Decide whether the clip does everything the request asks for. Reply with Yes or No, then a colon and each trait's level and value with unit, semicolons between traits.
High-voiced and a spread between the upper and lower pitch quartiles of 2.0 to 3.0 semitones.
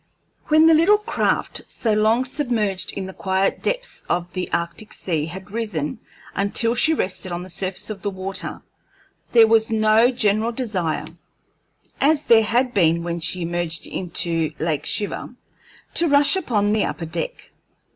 No: high, 205 Hz; average, 5.2 semitones